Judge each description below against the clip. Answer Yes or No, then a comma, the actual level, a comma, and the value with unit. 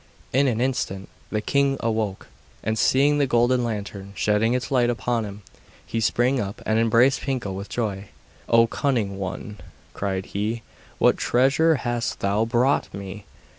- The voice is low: Yes, low, 115 Hz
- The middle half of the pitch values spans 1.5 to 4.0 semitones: Yes, average, 3.7 semitones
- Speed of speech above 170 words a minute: No, average, 155 wpm